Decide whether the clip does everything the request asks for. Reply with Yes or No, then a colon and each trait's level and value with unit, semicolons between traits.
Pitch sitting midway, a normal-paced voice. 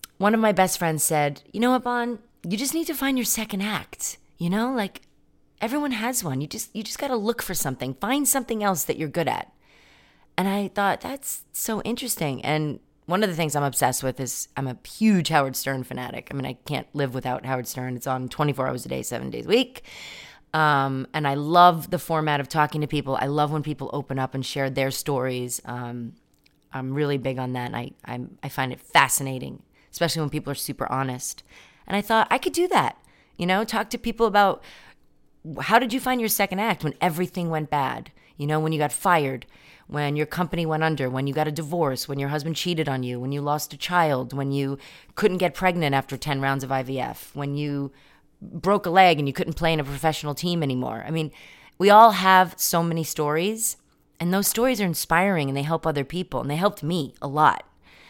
No: medium, 155 Hz; fast, 225 wpm